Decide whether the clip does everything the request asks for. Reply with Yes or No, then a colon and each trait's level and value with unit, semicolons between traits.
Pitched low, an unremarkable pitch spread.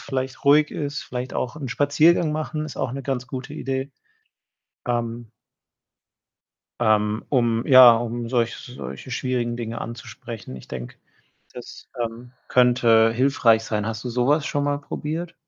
Yes: low, 125 Hz; average, 3.4 semitones